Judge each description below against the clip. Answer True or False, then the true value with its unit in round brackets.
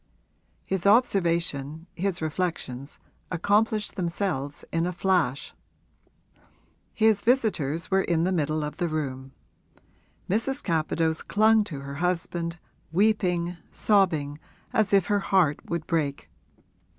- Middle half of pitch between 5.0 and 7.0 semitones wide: False (4.3 semitones)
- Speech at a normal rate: False (115 wpm)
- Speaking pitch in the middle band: True (170 Hz)